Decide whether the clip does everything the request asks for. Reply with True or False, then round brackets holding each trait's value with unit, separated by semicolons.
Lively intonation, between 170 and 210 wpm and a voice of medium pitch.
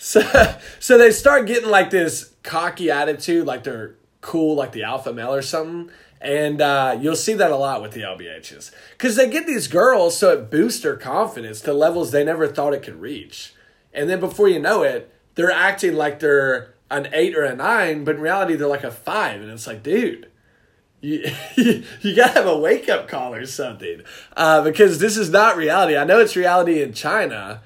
True (7.5 semitones; 205 wpm; 160 Hz)